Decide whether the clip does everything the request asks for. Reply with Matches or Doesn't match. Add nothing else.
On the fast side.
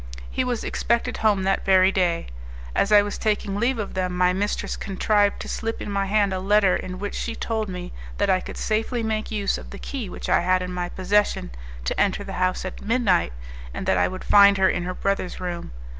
Matches